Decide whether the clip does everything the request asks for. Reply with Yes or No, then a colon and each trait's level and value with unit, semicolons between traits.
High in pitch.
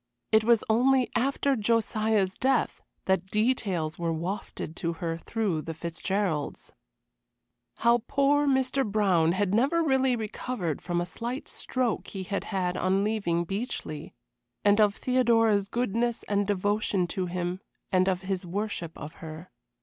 Yes: high, 205 Hz